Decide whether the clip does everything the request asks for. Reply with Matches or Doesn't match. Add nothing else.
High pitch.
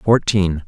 Doesn't match